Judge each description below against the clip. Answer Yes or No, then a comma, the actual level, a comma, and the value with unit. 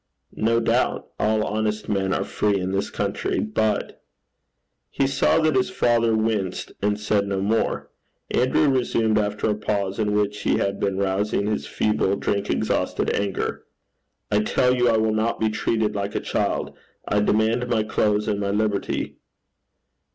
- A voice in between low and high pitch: No, low, 105 Hz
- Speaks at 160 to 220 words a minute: Yes, average, 165 wpm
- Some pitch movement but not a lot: No, narrow, 1.7 semitones